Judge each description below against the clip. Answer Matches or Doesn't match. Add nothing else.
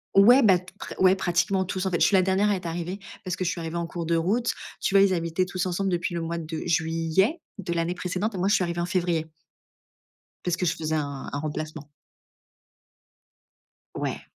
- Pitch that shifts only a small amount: Matches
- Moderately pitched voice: Matches